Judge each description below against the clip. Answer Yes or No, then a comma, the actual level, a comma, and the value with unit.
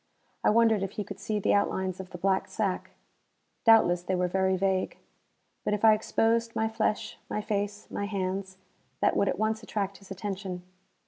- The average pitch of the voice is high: Yes, high, 200 Hz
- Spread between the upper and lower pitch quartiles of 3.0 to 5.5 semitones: No, narrow, 2.4 semitones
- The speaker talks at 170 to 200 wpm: Yes, average, 185 wpm